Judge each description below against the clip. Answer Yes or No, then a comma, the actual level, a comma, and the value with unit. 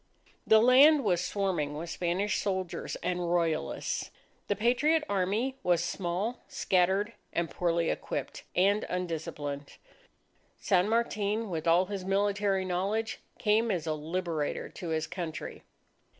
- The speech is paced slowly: Yes, slow, 125 wpm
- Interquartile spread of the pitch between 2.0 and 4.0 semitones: Yes, average, 3.5 semitones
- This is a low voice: No, medium, 185 Hz